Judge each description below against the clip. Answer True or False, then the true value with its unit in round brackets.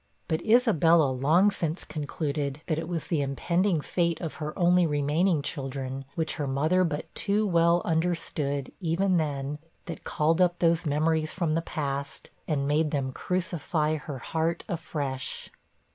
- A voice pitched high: False (160 Hz)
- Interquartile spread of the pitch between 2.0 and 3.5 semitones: True (3.0 semitones)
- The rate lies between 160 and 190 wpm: False (150 wpm)